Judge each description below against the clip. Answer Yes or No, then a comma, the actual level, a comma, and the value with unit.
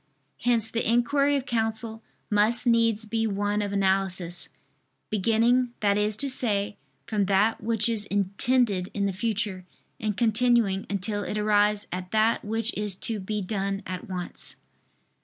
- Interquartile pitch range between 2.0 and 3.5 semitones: Yes, narrow, 2.4 semitones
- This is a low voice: No, high, 210 Hz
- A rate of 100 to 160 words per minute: Yes, average, 150 wpm